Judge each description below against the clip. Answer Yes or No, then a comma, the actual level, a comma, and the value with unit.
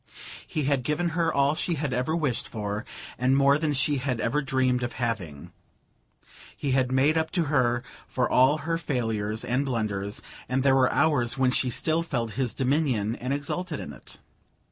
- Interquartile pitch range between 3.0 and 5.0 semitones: Yes, average, 3.7 semitones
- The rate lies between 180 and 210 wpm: Yes, average, 185 wpm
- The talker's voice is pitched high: No, low, 130 Hz